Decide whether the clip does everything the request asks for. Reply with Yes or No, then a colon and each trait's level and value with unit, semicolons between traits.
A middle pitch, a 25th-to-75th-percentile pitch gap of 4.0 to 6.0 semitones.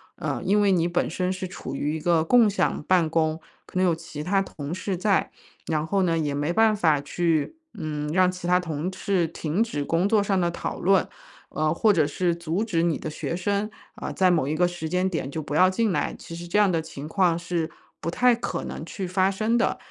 No: medium, 175 Hz; average, 3.3 semitones